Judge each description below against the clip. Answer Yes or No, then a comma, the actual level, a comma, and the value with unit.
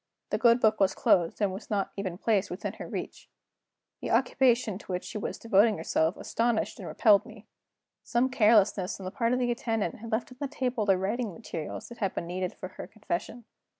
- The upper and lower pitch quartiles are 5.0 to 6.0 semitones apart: No, average, 3.8 semitones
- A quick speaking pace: Yes, fast, 210 wpm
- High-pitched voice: Yes, high, 215 Hz